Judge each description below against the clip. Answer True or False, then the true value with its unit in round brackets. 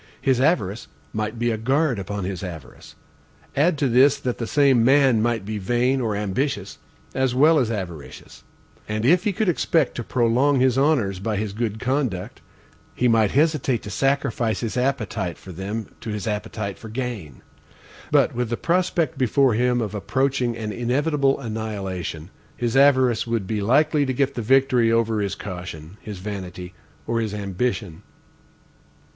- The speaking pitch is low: True (115 Hz)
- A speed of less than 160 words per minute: False (165 wpm)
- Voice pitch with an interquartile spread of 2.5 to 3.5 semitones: False (4.5 semitones)